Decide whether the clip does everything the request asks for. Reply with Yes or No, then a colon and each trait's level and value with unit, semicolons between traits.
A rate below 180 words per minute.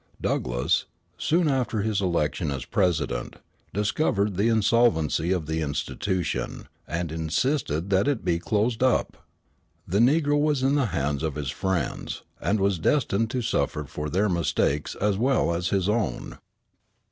Yes: average, 145 wpm